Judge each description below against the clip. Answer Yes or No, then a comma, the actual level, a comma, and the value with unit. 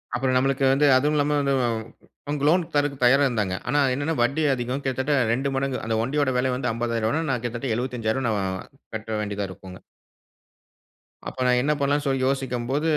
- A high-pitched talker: No, low, 130 Hz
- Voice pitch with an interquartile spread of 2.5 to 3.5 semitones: Yes, average, 3.1 semitones